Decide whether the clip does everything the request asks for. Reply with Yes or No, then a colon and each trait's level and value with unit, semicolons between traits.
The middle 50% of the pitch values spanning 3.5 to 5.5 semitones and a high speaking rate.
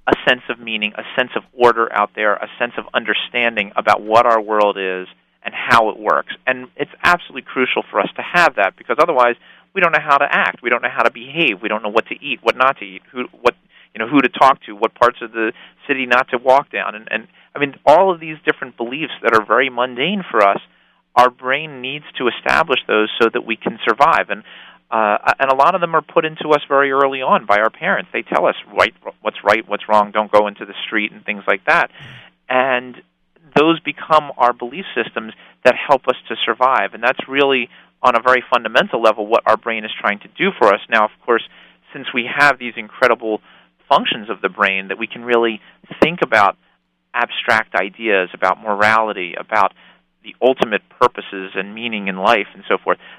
Yes: average, 4.1 semitones; fast, 220 wpm